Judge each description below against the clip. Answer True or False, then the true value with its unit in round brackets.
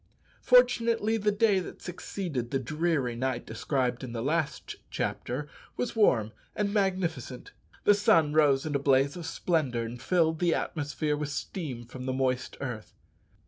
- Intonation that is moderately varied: False (5.9 semitones)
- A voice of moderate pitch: True (150 Hz)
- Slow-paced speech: False (155 wpm)